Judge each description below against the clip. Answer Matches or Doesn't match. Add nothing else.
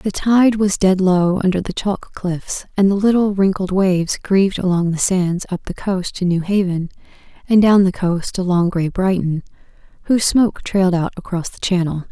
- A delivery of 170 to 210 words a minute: Matches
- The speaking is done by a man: Doesn't match